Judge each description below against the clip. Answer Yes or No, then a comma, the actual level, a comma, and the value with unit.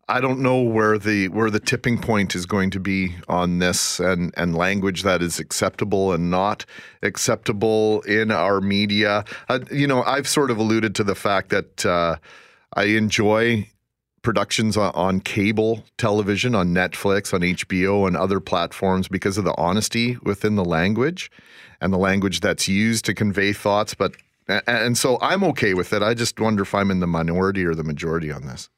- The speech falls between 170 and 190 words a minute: Yes, average, 185 wpm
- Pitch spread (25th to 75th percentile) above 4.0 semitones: No, average, 2.7 semitones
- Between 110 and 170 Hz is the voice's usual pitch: No, low, 100 Hz